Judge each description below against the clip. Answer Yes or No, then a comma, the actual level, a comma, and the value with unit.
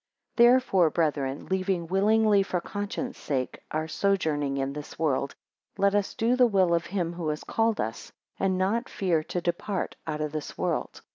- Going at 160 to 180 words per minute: Yes, average, 170 wpm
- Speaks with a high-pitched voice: No, medium, 180 Hz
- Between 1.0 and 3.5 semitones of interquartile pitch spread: No, average, 4.7 semitones